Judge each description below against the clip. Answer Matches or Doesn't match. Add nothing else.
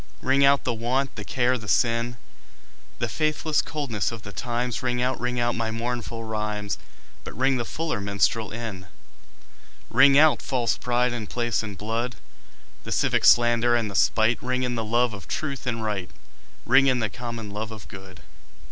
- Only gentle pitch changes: Matches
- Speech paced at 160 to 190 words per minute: Matches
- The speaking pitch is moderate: Doesn't match